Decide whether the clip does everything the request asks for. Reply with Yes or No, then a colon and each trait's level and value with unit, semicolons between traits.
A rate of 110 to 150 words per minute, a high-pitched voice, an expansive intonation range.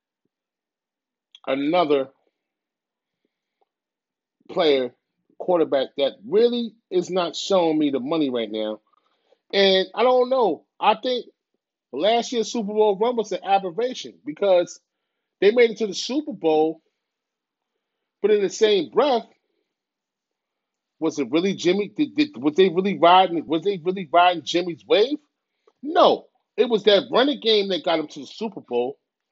Yes: average, 140 wpm; high, 195 Hz; wide, 6.8 semitones